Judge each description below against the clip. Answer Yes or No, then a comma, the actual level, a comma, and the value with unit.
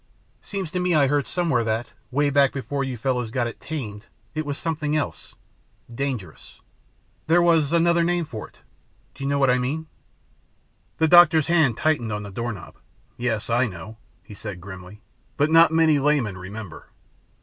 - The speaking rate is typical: Yes, average, 170 wpm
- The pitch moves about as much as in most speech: No, wide, 6.0 semitones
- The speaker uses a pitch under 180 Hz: Yes, medium, 140 Hz